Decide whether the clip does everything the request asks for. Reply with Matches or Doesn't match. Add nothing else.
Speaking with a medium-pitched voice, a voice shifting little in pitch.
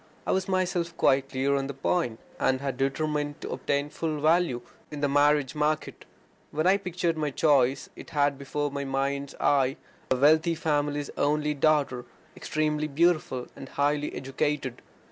Matches